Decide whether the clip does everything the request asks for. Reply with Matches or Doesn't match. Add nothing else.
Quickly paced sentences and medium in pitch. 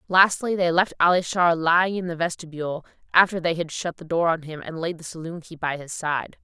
Matches